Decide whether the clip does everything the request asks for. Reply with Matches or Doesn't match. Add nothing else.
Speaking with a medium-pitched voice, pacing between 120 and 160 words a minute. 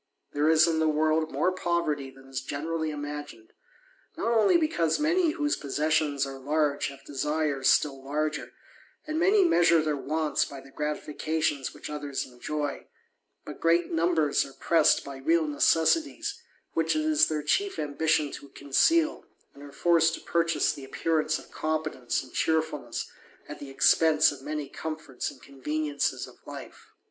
Matches